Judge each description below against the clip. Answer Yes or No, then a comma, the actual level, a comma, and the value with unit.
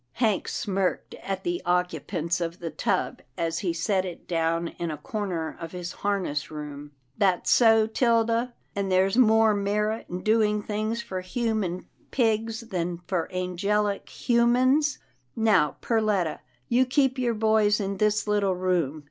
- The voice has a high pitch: Yes, high, 200 Hz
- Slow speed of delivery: No, average, 160 wpm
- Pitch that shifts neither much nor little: Yes, average, 4.0 semitones